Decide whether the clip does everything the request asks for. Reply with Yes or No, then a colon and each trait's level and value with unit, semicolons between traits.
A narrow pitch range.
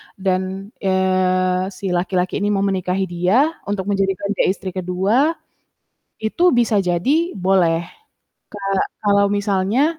Yes: narrow, 1.9 semitones